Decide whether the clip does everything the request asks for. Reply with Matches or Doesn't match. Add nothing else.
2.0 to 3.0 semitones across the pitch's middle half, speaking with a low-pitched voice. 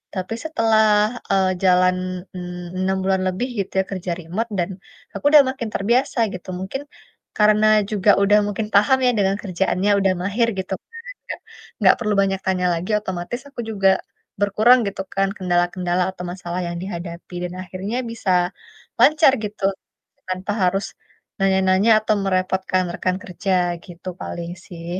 Doesn't match